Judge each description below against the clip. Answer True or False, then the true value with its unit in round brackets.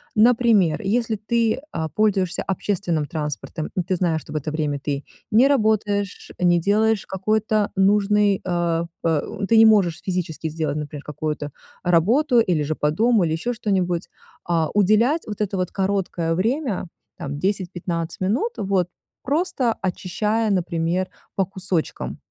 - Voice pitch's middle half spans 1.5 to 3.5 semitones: False (4.6 semitones)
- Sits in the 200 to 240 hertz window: False (190 Hz)